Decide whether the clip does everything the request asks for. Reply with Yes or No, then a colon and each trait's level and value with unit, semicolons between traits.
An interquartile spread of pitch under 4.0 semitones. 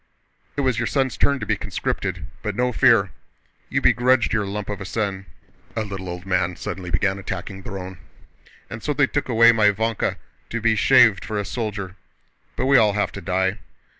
Yes: average, 3.4 semitones